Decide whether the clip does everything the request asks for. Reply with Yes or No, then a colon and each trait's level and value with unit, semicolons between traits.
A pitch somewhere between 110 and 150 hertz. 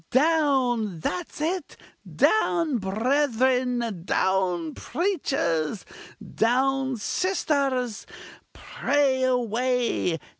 No: very high, 255 Hz